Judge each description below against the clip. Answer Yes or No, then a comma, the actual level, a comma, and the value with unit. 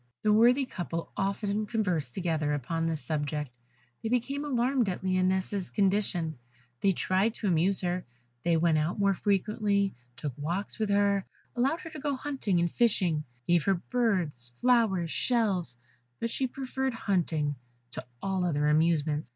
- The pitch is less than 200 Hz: Yes, high, 190 Hz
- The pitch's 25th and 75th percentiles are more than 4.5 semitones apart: Yes, average, 5.3 semitones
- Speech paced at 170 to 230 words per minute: No, average, 150 wpm